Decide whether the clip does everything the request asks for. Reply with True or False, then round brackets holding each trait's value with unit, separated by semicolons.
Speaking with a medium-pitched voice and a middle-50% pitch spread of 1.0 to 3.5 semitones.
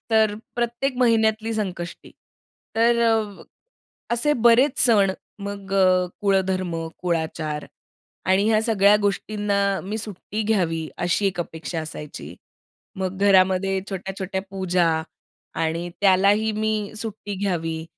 False (200 Hz; 2.9 semitones)